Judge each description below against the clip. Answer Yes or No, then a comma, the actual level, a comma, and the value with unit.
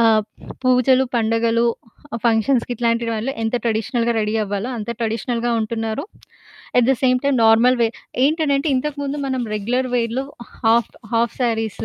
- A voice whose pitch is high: Yes, high, 235 Hz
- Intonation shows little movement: Yes, narrow, 2.3 semitones